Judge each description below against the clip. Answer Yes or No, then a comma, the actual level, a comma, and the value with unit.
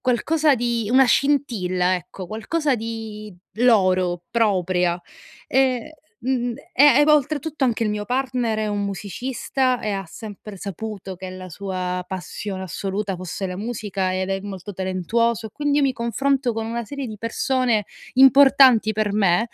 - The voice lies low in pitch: No, high, 220 Hz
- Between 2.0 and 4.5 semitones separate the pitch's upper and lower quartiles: No, average, 5.0 semitones